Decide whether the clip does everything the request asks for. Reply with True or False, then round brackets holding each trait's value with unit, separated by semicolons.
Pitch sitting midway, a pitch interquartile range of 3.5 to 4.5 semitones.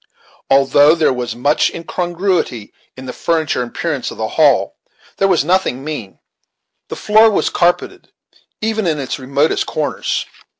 False (150 Hz; 5.1 semitones)